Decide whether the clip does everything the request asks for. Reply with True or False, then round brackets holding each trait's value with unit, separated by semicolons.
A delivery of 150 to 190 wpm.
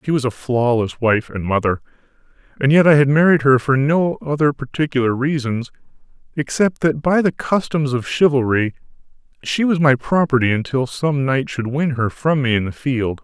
True (180 wpm)